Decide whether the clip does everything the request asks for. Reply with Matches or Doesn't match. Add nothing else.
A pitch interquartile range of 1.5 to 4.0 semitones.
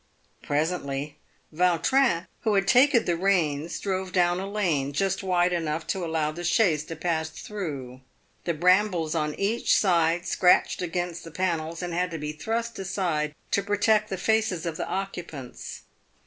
Matches